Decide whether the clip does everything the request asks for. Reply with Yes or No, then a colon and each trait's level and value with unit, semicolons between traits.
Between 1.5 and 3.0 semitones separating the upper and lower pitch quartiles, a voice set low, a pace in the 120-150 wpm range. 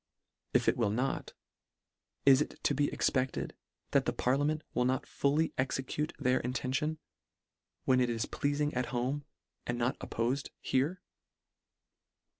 Yes: narrow, 2.5 semitones; low, 130 Hz; slow, 135 wpm